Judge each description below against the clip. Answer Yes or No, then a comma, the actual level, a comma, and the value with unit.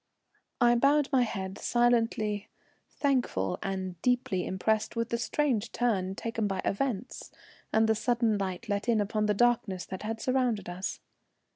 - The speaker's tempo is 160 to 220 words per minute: No, average, 150 wpm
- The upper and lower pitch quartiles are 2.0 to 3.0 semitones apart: No, average, 3.7 semitones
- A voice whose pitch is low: No, high, 220 Hz